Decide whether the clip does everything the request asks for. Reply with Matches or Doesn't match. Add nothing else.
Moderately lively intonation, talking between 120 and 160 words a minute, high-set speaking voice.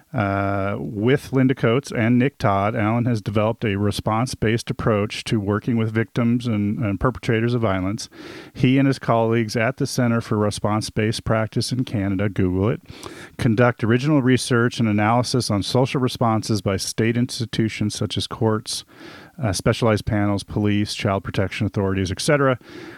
Doesn't match